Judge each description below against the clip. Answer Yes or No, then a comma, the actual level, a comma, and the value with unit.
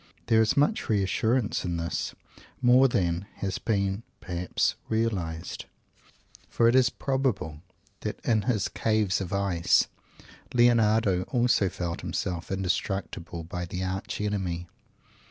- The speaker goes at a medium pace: No, slow, 120 wpm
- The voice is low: Yes, low, 100 Hz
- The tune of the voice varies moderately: Yes, average, 4.3 semitones